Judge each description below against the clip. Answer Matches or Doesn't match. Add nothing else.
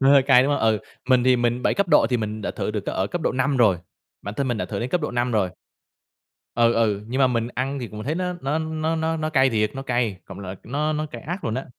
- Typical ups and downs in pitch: Matches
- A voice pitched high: Doesn't match